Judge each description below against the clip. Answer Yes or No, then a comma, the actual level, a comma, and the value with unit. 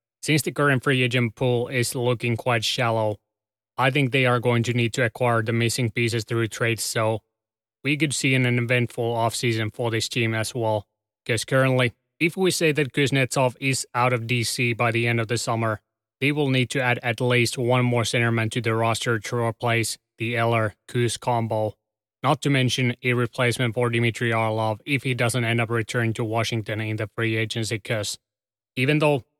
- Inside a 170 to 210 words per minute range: Yes, average, 195 wpm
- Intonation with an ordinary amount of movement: No, narrow, 2.0 semitones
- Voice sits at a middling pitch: No, low, 120 Hz